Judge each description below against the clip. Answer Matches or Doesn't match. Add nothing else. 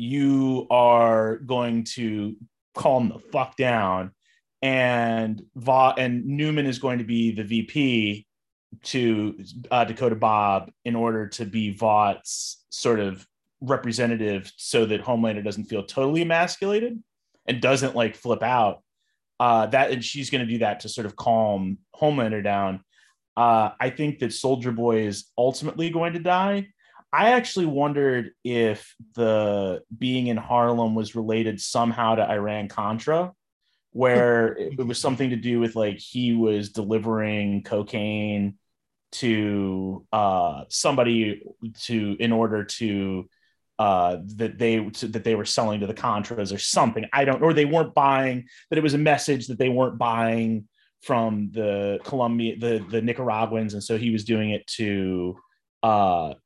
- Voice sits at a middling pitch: Doesn't match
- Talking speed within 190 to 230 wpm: Doesn't match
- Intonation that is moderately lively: Matches